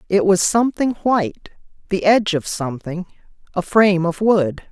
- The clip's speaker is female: Yes, female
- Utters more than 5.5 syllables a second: No, 5.4 syllables/s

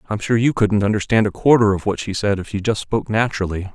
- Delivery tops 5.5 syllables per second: Yes, 6.5 syllables/s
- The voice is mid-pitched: No, low, 105 Hz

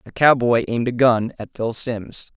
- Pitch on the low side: Yes, low, 120 Hz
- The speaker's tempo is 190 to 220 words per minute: Yes, average, 200 wpm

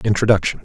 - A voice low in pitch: Yes, low, 100 Hz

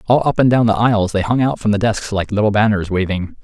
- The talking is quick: Yes, fast, 280 wpm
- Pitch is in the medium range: No, low, 105 Hz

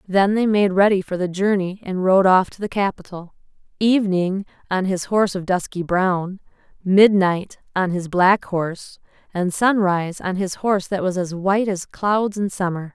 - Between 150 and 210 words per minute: Yes, average, 170 wpm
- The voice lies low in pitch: No, high, 190 Hz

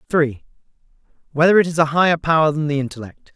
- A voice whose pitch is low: No, medium, 155 Hz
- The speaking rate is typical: Yes, average, 180 wpm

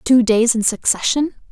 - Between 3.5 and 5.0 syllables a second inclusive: Yes, 4.9 syllables/s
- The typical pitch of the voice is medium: No, high, 240 Hz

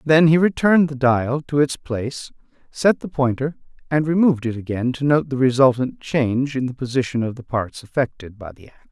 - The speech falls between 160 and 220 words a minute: Yes, average, 200 wpm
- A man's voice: Yes, male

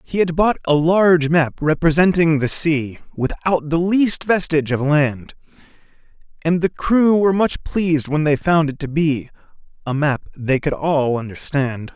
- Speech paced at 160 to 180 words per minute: Yes, average, 165 wpm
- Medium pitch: Yes, medium, 155 Hz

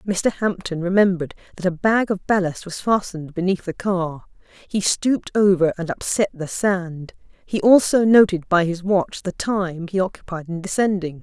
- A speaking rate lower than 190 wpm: Yes, average, 170 wpm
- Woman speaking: Yes, female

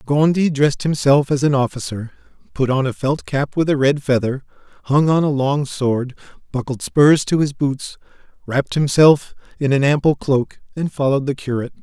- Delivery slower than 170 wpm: No, average, 180 wpm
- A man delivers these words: Yes, male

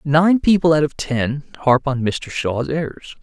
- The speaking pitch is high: No, medium, 150 Hz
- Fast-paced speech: No, average, 185 wpm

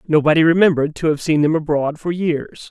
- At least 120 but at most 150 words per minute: No, average, 200 wpm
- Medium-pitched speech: Yes, medium, 160 Hz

